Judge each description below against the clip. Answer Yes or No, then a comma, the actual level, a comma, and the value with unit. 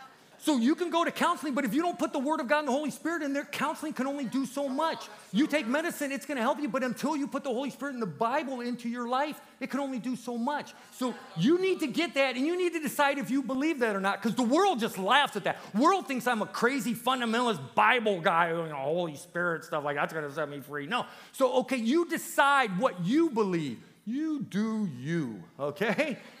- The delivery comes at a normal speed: No, fast, 245 wpm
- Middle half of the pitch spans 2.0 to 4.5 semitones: No, average, 5.0 semitones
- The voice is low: No, very high, 260 Hz